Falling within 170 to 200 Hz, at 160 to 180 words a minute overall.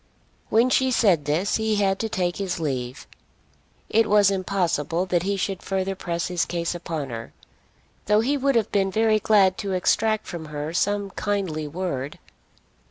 Yes: high, 190 Hz; average, 165 wpm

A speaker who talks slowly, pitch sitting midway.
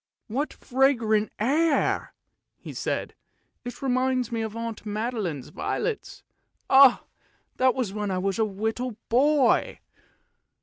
No: slow, 120 wpm; high, 235 Hz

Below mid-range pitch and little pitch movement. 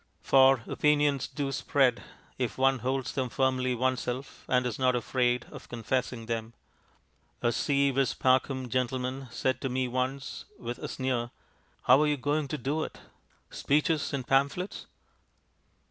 Yes: low, 130 Hz; narrow, 1.7 semitones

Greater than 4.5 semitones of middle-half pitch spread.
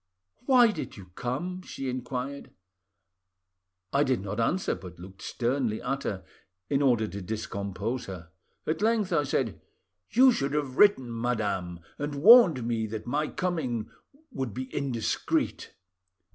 Yes: average, 5.3 semitones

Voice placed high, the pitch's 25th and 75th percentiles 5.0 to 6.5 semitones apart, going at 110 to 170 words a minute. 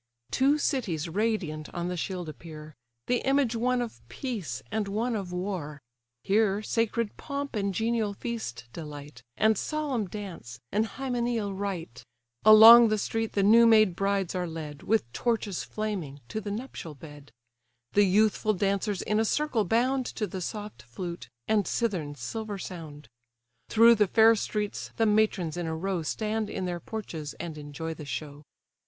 Yes: high, 205 Hz; average, 5.3 semitones; average, 160 wpm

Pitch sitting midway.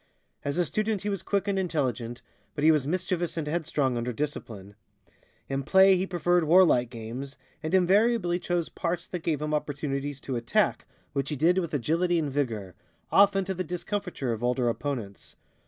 Yes: medium, 155 Hz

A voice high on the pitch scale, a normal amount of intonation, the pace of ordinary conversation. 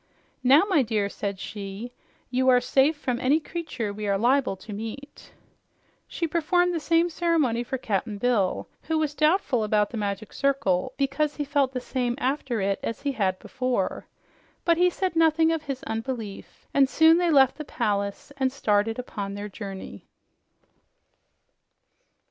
No: very high, 255 Hz; wide, 6.2 semitones; average, 160 wpm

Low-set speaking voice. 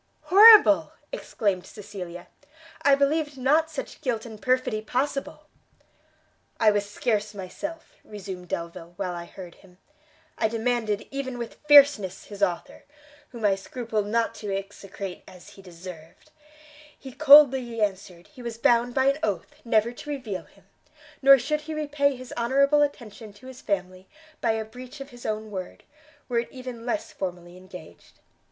No: high, 225 Hz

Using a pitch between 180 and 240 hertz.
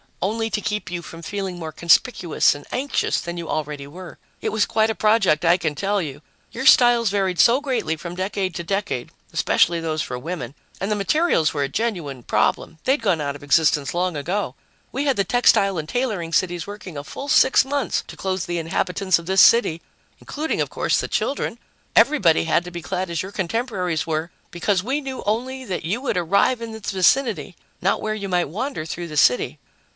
Yes: medium, 185 Hz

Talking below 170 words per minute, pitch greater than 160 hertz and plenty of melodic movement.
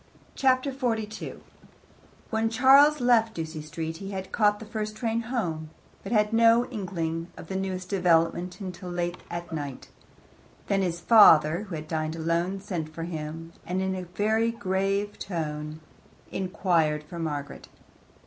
No: average, 145 wpm; medium, 185 Hz; average, 4.8 semitones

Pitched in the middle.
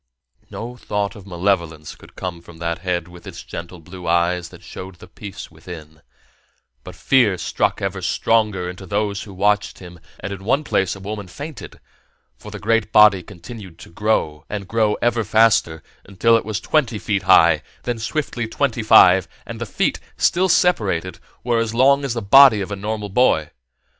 No: low, 100 Hz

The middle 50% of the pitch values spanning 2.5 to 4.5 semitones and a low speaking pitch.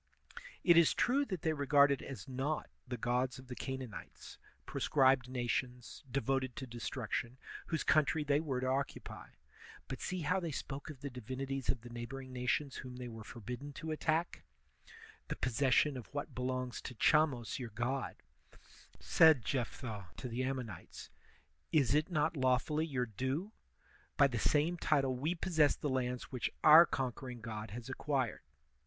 Yes: average, 3.1 semitones; low, 130 Hz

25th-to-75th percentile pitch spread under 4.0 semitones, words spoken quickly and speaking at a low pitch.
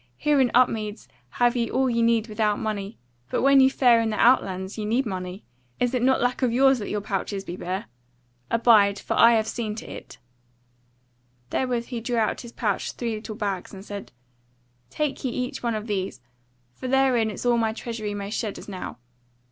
No: average, 3.0 semitones; fast, 210 wpm; high, 230 Hz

